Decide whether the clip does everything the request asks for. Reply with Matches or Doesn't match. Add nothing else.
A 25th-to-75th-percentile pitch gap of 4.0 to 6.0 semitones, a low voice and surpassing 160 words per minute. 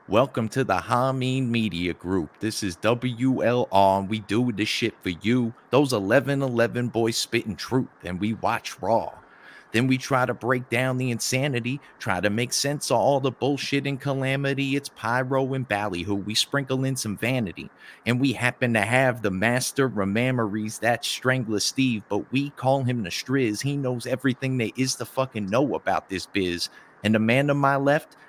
Doesn't match